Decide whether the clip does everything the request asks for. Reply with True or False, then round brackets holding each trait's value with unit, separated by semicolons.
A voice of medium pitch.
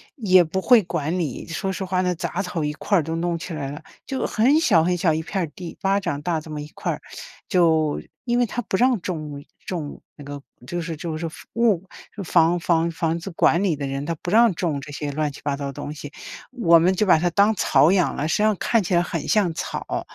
True (170 Hz)